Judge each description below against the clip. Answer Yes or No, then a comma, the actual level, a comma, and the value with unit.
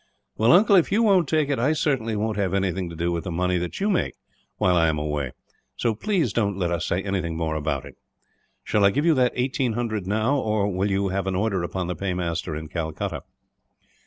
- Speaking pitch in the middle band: No, low, 100 Hz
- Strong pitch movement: Yes, wide, 6.0 semitones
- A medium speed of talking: No, fast, 225 wpm